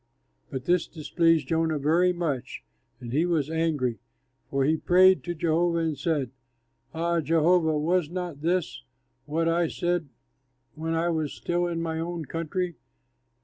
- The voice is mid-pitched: Yes, medium, 165 Hz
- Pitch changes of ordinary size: No, narrow, 2.2 semitones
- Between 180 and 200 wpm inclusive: No, average, 145 wpm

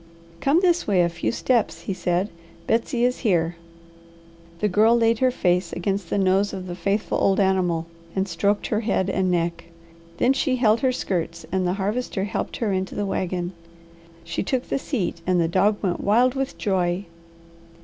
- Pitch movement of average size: Yes, average, 4.2 semitones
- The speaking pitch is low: No, high, 195 Hz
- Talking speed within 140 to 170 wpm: No, average, 180 wpm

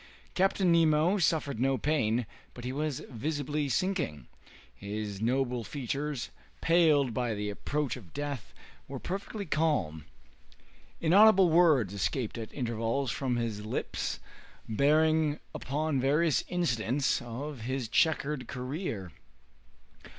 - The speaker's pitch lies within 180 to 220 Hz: No, medium, 140 Hz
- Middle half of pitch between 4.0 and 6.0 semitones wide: Yes, average, 5.1 semitones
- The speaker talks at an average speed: No, slow, 115 wpm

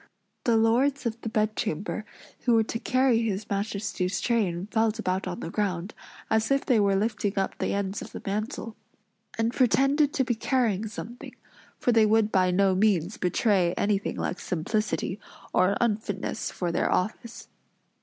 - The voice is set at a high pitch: Yes, high, 215 Hz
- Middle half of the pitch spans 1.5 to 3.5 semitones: Yes, average, 2.9 semitones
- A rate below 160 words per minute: No, average, 165 wpm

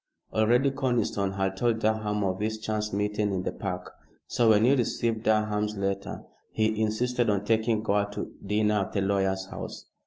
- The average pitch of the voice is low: Yes, low, 105 Hz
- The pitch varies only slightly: Yes, narrow, 1.9 semitones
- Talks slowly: No, average, 175 wpm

